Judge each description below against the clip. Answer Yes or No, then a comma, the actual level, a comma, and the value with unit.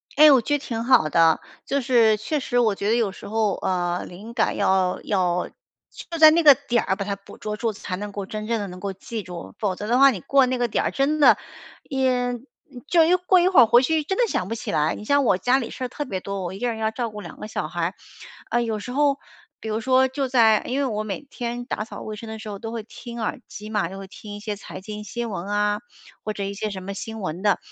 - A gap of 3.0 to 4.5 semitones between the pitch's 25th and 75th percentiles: Yes, average, 4.1 semitones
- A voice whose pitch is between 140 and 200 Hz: No, high, 220 Hz